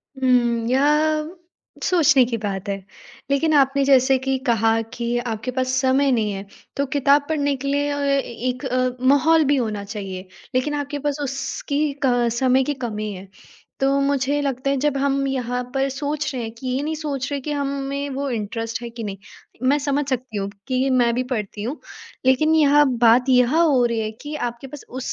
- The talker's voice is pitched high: Yes, very high, 265 Hz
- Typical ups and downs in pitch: Yes, average, 3.0 semitones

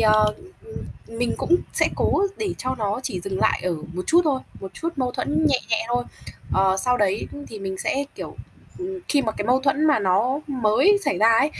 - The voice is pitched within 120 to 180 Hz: No, high, 245 Hz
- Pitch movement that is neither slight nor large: No, wide, 5.8 semitones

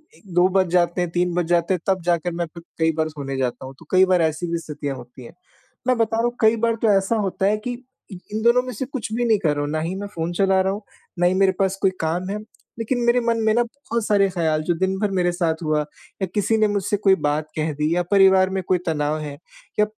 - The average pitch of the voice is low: No, medium, 185 Hz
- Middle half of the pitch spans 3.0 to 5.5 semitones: Yes, average, 4.2 semitones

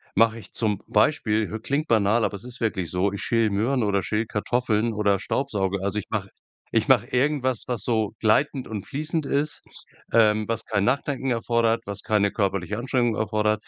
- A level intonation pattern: No, average, 3.1 semitones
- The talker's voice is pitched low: Yes, low, 110 Hz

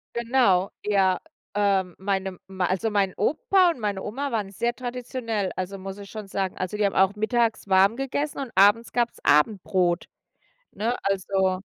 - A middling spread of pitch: Yes, average, 3.7 semitones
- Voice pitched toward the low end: No, high, 200 Hz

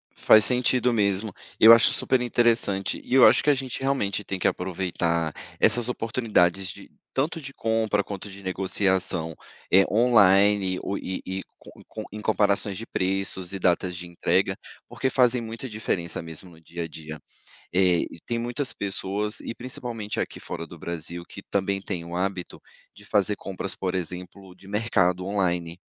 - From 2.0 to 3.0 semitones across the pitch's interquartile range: No, average, 3.8 semitones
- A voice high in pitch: No, low, 100 Hz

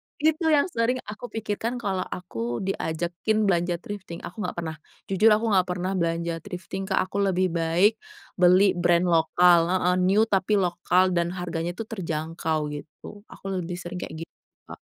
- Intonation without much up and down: No, average, 3.0 semitones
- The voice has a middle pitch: Yes, medium, 180 Hz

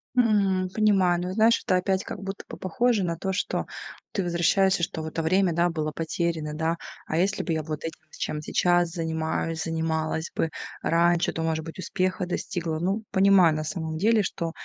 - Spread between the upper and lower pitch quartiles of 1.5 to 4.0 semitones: Yes, average, 2.9 semitones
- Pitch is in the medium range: Yes, medium, 170 Hz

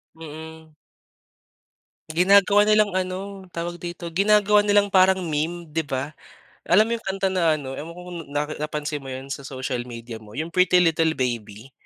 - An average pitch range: Yes, average, 4.8 semitones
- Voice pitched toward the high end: No, medium, 165 Hz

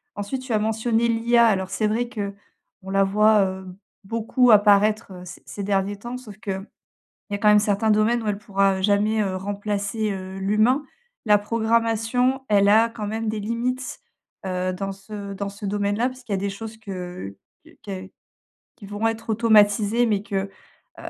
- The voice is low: No, high, 210 Hz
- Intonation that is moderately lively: No, narrow, 2.3 semitones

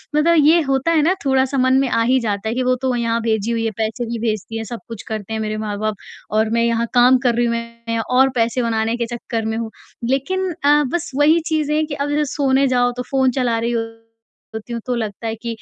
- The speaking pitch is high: Yes, high, 235 Hz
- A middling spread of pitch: Yes, average, 3.0 semitones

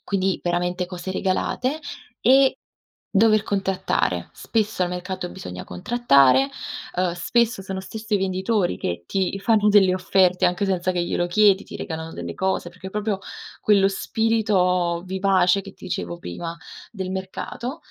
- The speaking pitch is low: No, high, 190 Hz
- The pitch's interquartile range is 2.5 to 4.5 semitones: Yes, average, 2.8 semitones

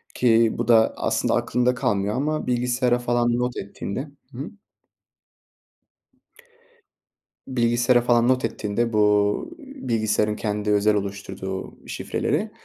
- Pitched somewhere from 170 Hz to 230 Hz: No, low, 120 Hz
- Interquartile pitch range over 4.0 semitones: No, average, 3.0 semitones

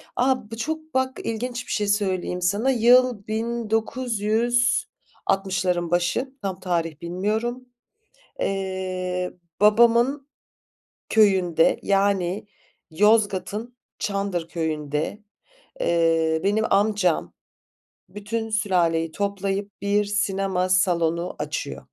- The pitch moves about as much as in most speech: Yes, average, 3.9 semitones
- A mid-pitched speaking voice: No, high, 200 Hz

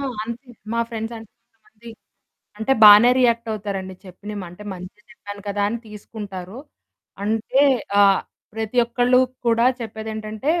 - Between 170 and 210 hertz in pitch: No, high, 220 Hz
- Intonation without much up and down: Yes, narrow, 2.3 semitones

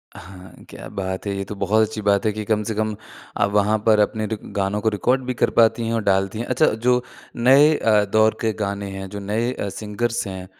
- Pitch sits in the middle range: No, low, 105 Hz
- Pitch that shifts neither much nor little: No, narrow, 2.2 semitones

